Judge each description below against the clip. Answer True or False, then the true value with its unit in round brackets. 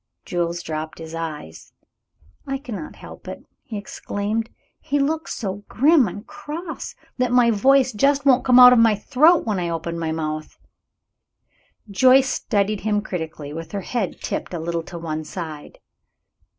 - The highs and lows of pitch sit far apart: True (7.4 semitones)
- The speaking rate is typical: True (160 wpm)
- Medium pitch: False (205 Hz)